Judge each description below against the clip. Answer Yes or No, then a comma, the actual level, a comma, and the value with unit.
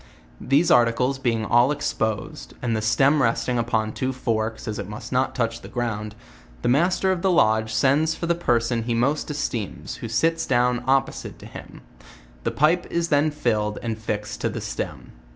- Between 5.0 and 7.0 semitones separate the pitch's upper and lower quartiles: No, average, 4.3 semitones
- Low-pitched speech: Yes, low, 120 Hz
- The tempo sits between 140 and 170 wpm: No, average, 190 wpm